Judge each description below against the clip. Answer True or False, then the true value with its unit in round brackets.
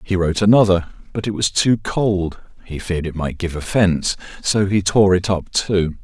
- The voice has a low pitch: True (95 Hz)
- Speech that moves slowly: False (200 wpm)